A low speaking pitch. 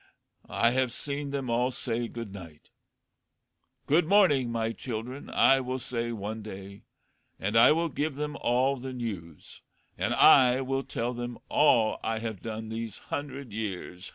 Yes: low, 120 Hz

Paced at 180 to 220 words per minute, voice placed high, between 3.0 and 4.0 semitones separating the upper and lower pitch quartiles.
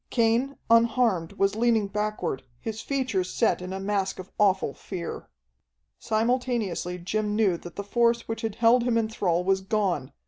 No: average, 165 wpm; high, 210 Hz; average, 3.3 semitones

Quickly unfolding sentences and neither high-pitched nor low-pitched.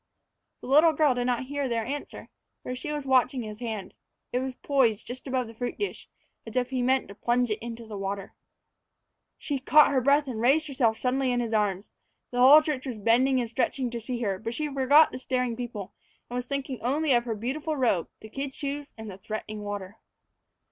No: fast, 215 wpm; very high, 250 Hz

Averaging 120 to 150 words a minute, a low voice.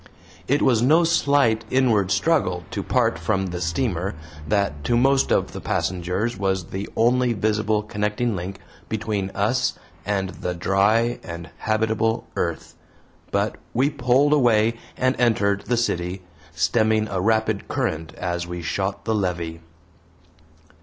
Yes: average, 140 wpm; low, 105 Hz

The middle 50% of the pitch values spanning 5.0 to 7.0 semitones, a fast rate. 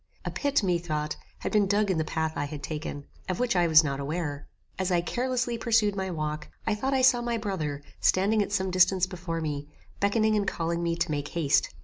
Yes: average, 5.3 semitones; fast, 220 wpm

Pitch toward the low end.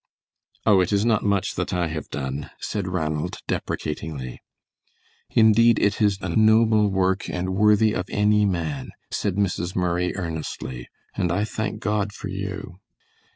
Yes: very low, 95 Hz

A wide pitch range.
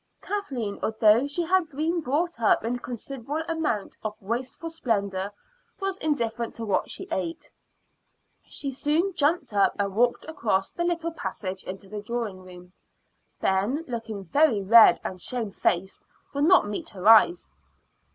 Yes: wide, 7.4 semitones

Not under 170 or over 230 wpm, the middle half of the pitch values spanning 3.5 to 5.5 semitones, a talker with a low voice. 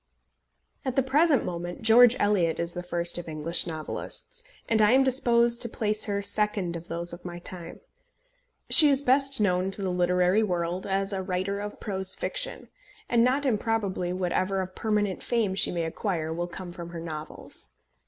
No: average, 180 wpm; average, 4.4 semitones; high, 190 Hz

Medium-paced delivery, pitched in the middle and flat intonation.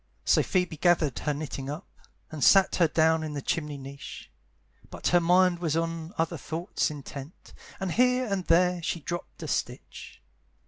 No: average, 170 wpm; medium, 165 Hz; average, 3.0 semitones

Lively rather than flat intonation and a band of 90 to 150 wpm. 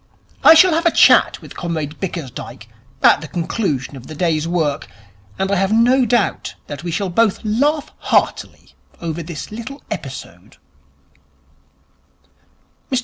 Yes: wide, 6.9 semitones; average, 140 wpm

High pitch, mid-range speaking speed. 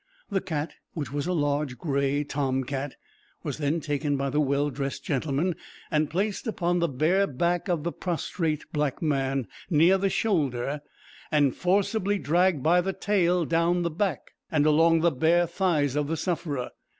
No: medium, 155 Hz; average, 170 wpm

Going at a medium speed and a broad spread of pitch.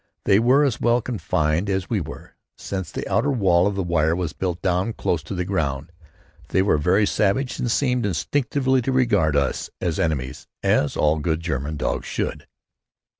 Yes: average, 175 wpm; wide, 6.7 semitones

